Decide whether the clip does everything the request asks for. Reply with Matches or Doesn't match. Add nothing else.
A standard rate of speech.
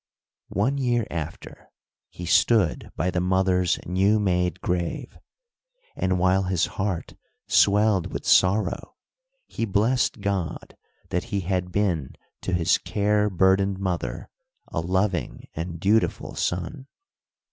Doesn't match